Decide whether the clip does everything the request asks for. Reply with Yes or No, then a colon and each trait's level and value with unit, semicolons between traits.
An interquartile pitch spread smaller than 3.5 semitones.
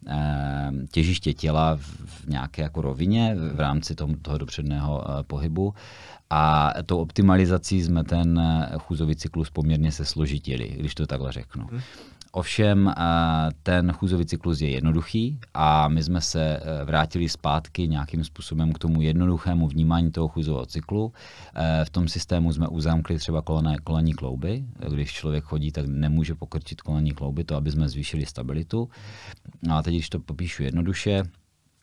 Yes: narrow, 2.4 semitones